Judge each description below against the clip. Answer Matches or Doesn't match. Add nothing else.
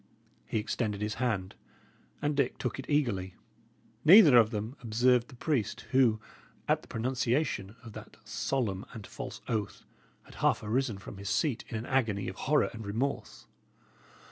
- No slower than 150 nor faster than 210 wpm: Matches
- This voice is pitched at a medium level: Doesn't match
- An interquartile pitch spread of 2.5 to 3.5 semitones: Doesn't match